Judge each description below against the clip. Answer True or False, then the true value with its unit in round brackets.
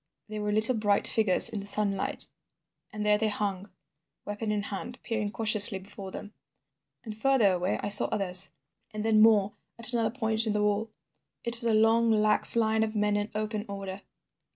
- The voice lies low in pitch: False (210 Hz)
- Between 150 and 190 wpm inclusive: True (185 wpm)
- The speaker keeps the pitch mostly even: True (1.4 semitones)